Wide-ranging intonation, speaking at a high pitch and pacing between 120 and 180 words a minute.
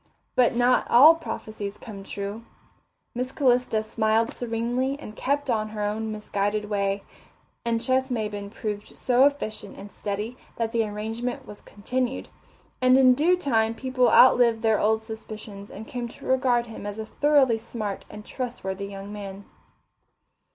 No: average, 3.1 semitones; high, 225 Hz; average, 150 wpm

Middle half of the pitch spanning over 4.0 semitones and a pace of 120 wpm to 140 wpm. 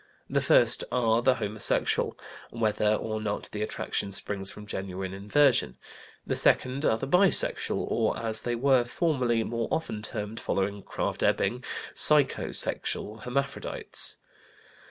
No: average, 3.5 semitones; slow, 135 wpm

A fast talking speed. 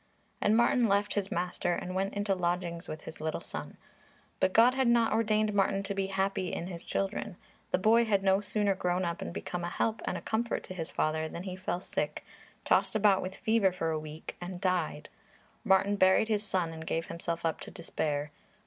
Yes: fast, 210 wpm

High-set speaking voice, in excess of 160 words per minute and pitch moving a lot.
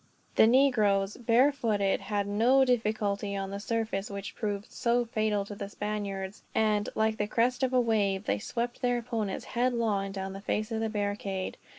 No: high, 215 Hz; average, 175 wpm; average, 2.8 semitones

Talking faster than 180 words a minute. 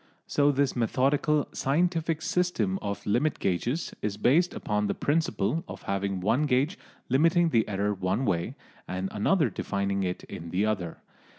No: average, 155 wpm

